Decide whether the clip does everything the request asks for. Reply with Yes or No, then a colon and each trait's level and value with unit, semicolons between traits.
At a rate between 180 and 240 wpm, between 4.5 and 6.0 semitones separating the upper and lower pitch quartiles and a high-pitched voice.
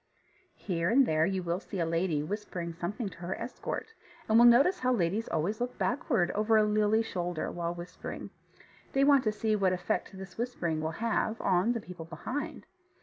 Yes: average, 190 wpm; average, 5.0 semitones; high, 200 Hz